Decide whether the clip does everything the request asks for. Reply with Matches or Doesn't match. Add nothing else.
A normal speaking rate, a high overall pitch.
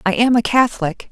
Doesn't match